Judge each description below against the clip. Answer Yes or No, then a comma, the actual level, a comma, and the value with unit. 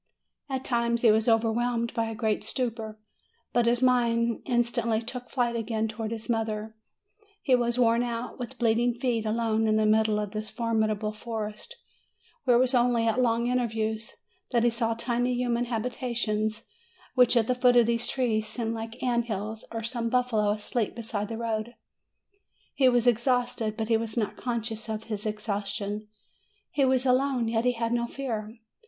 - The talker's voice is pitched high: Yes, high, 230 Hz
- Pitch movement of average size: No, narrow, 1.8 semitones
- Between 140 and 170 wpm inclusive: No, average, 180 wpm